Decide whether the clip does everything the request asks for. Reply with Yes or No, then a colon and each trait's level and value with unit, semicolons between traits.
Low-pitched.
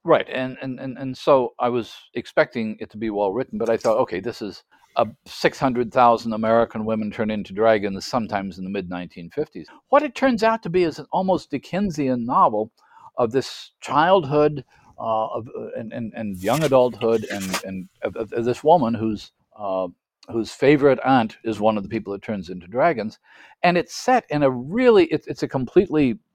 Yes: low, 120 Hz